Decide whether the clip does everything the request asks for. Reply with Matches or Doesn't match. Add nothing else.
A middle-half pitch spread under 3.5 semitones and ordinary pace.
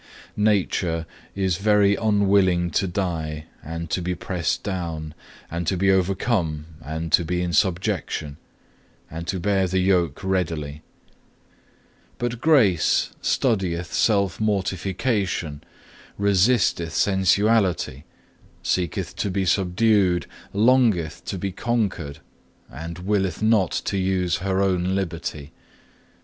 Doesn't match